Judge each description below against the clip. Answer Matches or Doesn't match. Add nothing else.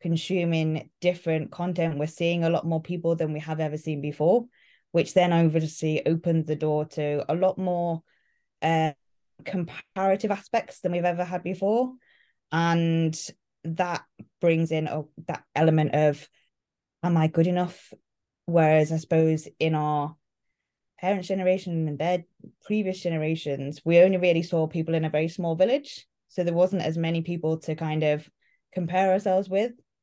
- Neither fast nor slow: Matches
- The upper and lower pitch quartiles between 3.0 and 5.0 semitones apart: Doesn't match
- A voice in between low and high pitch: Matches